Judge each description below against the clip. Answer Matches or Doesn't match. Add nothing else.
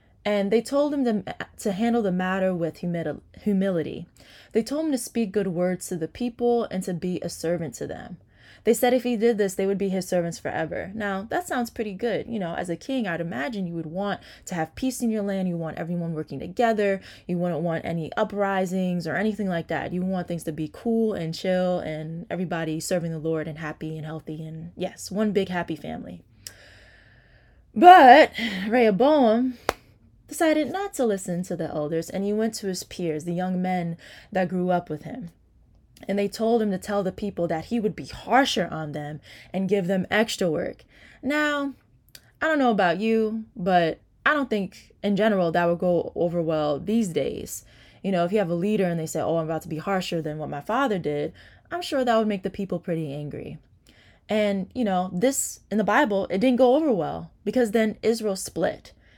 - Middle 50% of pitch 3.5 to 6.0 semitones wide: Matches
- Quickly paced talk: Matches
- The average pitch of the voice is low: Doesn't match